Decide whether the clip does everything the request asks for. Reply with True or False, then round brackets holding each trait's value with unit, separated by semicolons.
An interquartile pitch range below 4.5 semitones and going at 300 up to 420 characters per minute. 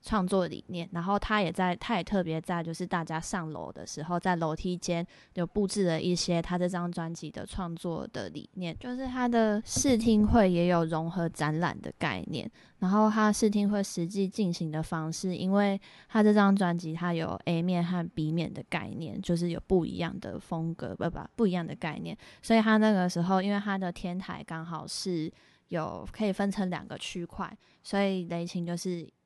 False (3.0 semitones; 285 characters per minute)